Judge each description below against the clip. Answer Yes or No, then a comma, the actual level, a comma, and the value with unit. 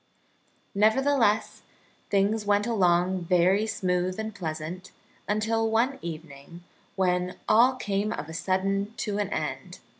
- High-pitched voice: Yes, high, 200 Hz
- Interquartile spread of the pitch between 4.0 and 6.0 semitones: No, average, 3.4 semitones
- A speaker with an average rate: No, slow, 120 wpm